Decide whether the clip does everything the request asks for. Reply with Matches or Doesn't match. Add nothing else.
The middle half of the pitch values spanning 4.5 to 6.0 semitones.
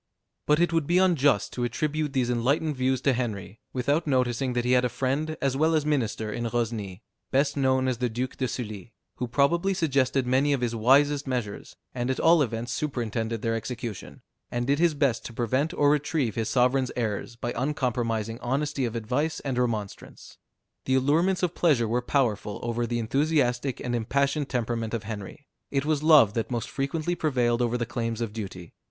Doesn't match